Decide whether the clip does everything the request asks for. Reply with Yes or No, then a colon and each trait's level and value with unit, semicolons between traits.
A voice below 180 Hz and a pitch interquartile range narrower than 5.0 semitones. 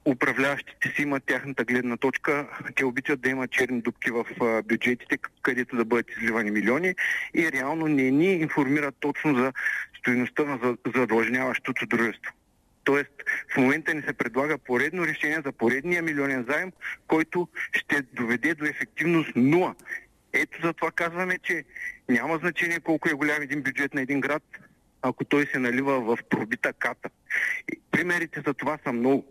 Yes: medium, 140 Hz; average, 3.4 semitones